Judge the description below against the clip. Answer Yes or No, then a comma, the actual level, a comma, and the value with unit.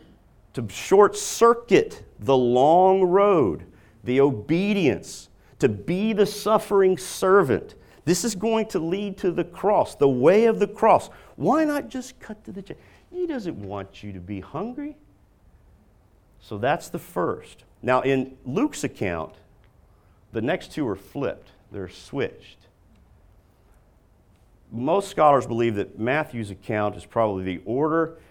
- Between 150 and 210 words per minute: No, slow, 135 wpm